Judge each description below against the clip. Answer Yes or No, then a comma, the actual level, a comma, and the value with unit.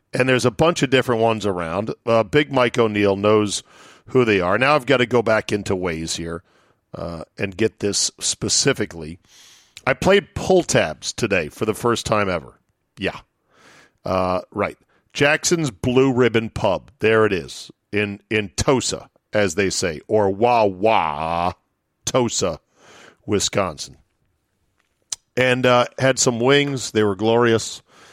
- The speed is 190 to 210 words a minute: No, average, 145 wpm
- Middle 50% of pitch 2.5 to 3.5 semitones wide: No, average, 4.3 semitones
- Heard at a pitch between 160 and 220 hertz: No, low, 110 Hz